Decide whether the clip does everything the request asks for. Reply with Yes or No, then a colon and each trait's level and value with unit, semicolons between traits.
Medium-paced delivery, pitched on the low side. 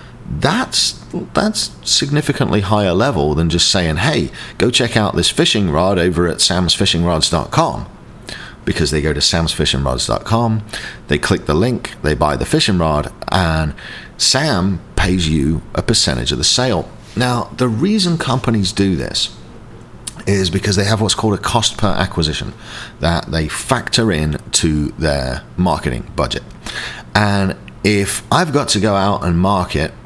Yes: average, 150 wpm; very low, 95 Hz